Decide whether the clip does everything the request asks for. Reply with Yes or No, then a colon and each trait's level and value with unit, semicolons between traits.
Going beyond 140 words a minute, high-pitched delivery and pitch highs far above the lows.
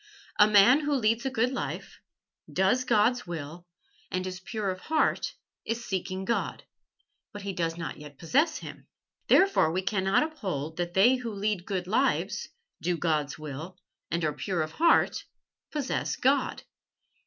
Yes: average, 155 wpm; high, 195 Hz; wide, 6.1 semitones